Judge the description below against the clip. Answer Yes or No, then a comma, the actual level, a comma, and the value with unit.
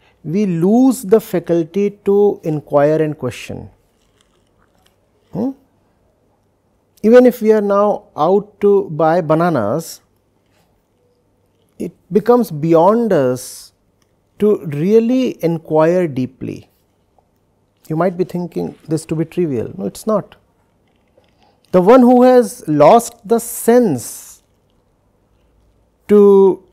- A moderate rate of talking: No, slow, 100 wpm